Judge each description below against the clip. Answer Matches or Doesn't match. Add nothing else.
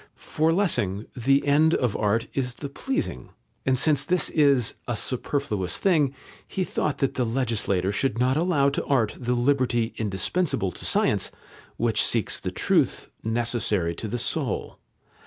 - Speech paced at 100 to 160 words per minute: Matches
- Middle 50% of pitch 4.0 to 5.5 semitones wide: Matches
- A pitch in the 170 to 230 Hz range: Doesn't match